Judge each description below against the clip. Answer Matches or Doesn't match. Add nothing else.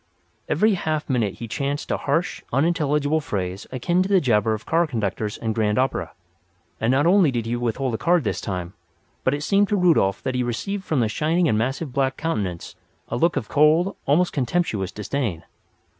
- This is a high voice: Doesn't match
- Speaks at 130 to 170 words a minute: Doesn't match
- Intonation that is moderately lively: Doesn't match